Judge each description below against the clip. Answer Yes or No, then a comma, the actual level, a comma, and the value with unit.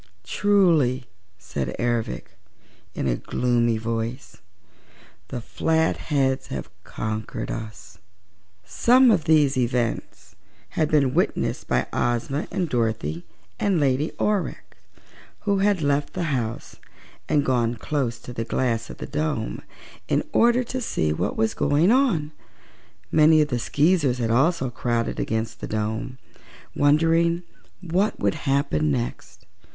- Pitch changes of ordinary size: No, wide, 5.9 semitones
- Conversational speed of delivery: No, slow, 125 wpm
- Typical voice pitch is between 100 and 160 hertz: Yes, low, 135 Hz